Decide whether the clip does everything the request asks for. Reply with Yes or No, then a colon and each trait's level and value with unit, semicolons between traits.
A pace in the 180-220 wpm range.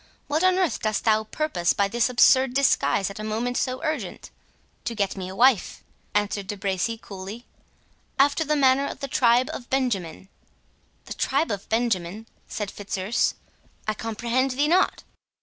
No: average, 165 wpm